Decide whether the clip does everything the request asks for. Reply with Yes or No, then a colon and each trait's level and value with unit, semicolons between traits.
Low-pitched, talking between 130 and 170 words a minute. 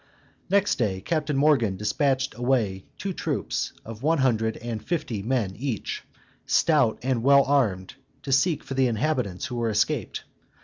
Yes: low, 125 Hz; average, 150 wpm